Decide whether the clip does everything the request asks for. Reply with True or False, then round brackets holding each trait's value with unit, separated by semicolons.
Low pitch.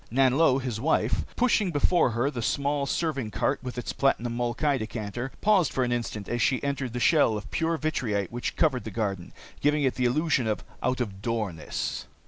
True (125 Hz)